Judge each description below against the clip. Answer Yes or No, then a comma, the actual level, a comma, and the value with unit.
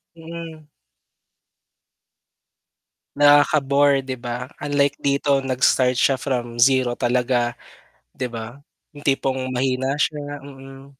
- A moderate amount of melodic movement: No, narrow, 2.2 semitones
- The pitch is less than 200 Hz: Yes, low, 135 Hz